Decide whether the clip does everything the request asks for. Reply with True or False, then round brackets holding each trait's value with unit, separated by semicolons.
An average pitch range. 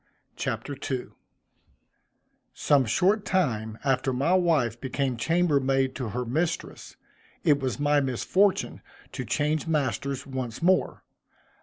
True (4.1 semitones)